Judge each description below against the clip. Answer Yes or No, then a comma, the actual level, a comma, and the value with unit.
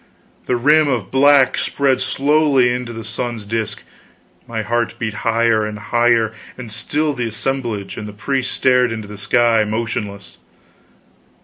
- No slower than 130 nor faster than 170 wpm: Yes, average, 145 wpm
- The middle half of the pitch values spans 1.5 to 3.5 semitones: Yes, average, 3.1 semitones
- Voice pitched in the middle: No, low, 120 Hz